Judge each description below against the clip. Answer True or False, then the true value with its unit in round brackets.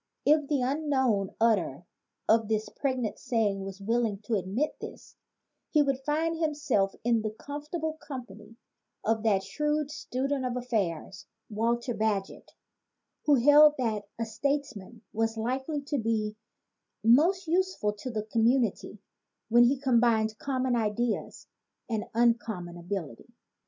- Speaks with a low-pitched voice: False (235 Hz)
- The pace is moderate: False (130 wpm)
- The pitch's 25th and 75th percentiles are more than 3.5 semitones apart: True (4.8 semitones)